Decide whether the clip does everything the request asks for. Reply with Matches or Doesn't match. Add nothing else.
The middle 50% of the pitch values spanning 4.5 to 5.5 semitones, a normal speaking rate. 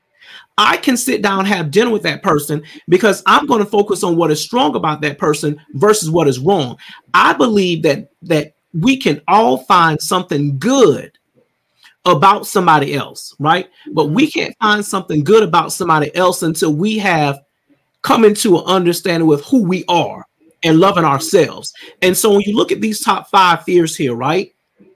Matches